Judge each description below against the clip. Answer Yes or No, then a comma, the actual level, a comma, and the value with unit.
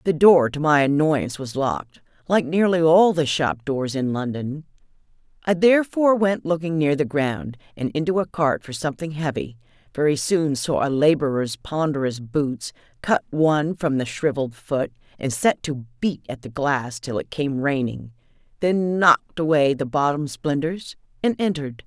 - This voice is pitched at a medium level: Yes, medium, 150 Hz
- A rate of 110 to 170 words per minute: Yes, average, 165 wpm